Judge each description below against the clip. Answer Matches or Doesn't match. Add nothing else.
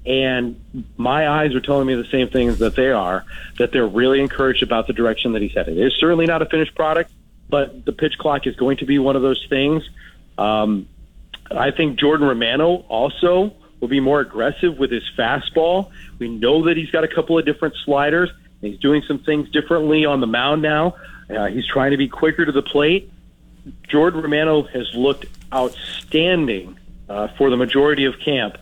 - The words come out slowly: Doesn't match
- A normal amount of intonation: Matches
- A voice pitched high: Doesn't match